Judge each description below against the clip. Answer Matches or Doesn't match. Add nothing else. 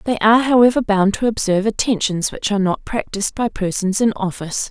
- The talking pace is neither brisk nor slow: Matches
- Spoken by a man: Doesn't match